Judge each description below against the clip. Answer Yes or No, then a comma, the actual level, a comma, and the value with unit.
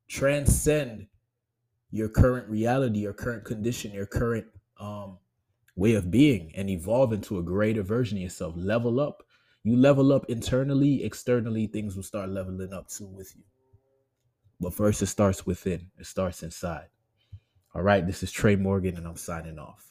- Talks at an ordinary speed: Yes, average, 165 wpm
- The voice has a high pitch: No, low, 105 Hz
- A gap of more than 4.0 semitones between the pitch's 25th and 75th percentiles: No, average, 3.7 semitones